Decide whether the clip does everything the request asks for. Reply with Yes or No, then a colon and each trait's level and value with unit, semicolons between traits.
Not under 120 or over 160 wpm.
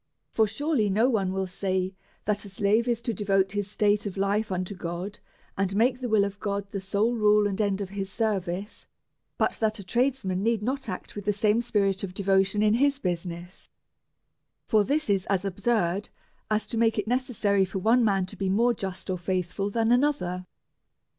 No: average, 195 wpm